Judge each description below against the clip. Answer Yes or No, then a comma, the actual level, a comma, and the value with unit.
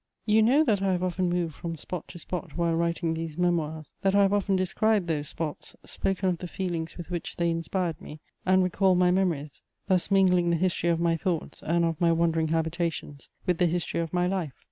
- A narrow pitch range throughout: Yes, narrow, 2.1 semitones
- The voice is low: No, medium, 175 Hz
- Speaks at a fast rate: Yes, fast, 215 wpm